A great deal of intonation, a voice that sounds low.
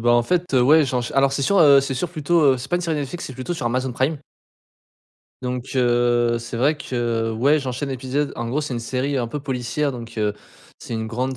No: average, 3.2 semitones; low, 130 Hz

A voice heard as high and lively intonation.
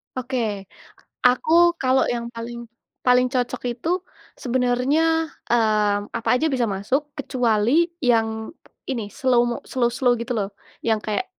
No: high, 245 Hz; narrow, 2.5 semitones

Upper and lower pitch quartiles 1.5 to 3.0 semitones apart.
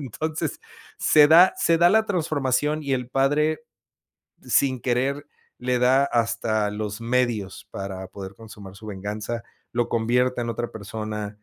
No: average, 4.8 semitones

